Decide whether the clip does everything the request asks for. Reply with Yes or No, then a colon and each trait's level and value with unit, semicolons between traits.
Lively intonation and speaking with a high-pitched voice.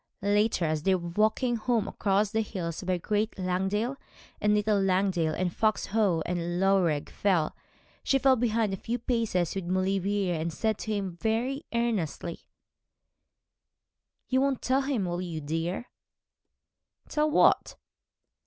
No: average, 4.1 semitones; high, 195 Hz